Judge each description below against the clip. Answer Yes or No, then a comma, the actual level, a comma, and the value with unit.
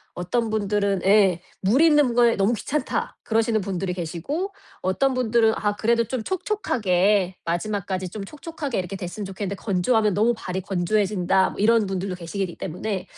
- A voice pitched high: Yes, high, 205 Hz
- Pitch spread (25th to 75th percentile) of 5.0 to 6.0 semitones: No, average, 3.7 semitones